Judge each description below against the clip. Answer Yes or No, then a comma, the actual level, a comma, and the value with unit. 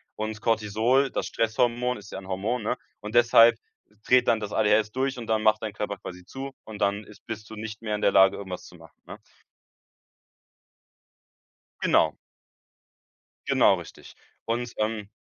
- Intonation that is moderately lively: No, narrow, 2.1 semitones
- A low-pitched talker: Yes, low, 110 Hz